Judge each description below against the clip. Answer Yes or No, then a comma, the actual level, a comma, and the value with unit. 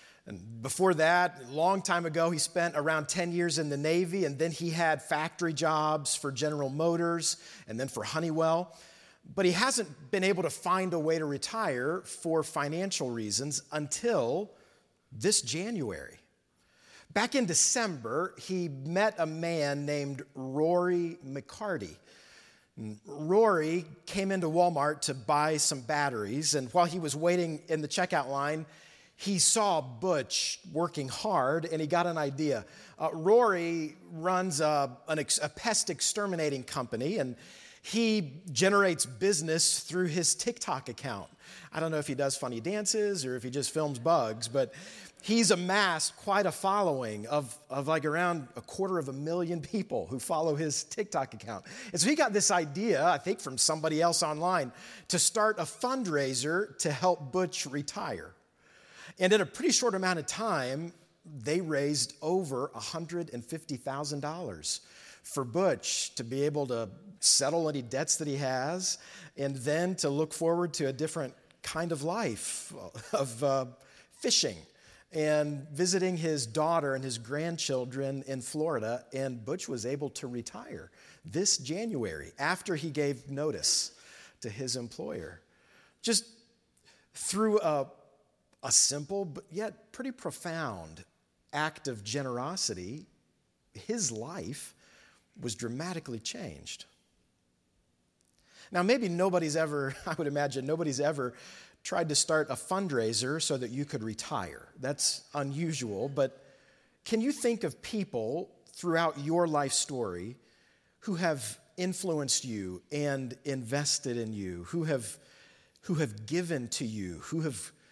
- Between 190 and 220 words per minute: No, average, 145 wpm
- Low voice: No, medium, 160 Hz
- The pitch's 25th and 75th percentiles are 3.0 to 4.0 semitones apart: No, average, 4.4 semitones